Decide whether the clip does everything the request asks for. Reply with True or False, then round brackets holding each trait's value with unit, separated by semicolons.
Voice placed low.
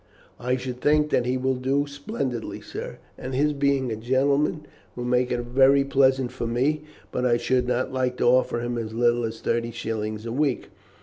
True (125 Hz)